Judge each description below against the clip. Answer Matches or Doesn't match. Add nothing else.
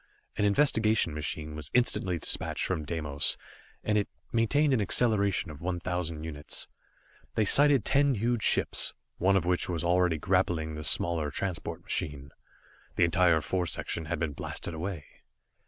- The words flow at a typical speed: Matches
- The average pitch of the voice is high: Doesn't match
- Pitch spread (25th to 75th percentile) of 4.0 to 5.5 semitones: Matches